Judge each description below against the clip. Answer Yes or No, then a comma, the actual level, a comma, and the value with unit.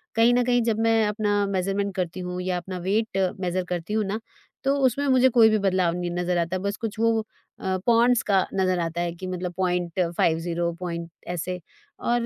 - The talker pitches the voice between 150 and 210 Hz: Yes, medium, 185 Hz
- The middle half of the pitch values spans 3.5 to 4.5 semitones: Yes, average, 4.0 semitones